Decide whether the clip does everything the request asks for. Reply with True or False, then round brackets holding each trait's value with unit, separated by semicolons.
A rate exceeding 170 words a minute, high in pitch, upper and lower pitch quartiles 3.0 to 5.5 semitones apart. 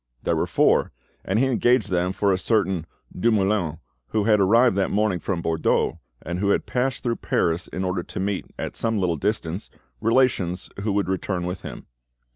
False (185 wpm; 95 Hz; 3.4 semitones)